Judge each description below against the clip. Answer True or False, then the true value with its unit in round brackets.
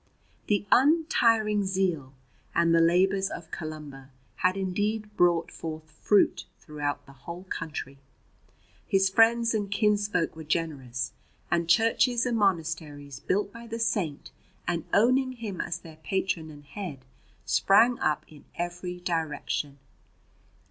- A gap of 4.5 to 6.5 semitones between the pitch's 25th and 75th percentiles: True (4.9 semitones)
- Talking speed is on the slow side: True (125 wpm)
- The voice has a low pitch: False (180 Hz)